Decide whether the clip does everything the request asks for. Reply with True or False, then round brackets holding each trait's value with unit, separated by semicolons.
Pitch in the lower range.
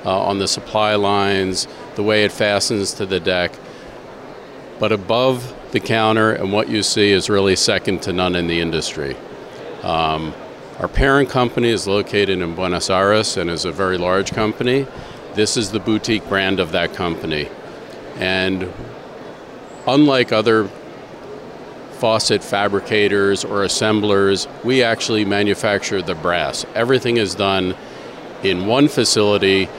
True (100 Hz)